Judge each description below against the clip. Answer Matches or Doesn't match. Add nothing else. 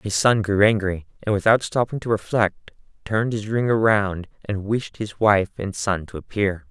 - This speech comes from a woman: Doesn't match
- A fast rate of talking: Doesn't match